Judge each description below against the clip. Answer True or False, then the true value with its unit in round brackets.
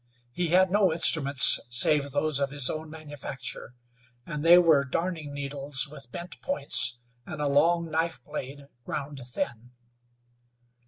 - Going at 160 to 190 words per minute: False (140 wpm)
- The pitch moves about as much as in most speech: True (3.0 semitones)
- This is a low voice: False (145 Hz)